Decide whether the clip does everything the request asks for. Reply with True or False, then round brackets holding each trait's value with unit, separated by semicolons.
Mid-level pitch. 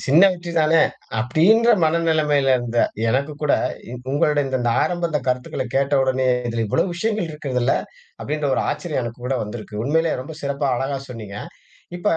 True (145 Hz)